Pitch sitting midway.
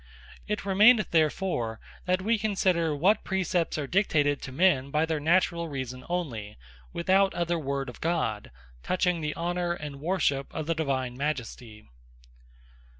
Yes: medium, 160 Hz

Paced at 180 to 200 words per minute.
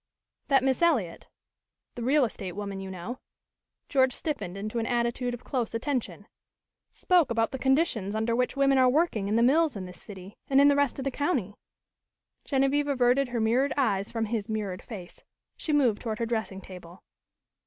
Yes: average, 190 wpm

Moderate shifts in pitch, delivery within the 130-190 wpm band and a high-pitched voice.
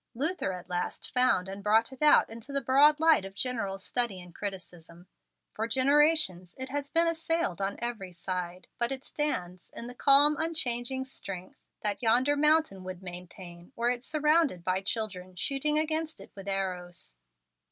No: wide, 7.6 semitones; average, 165 wpm; high, 230 Hz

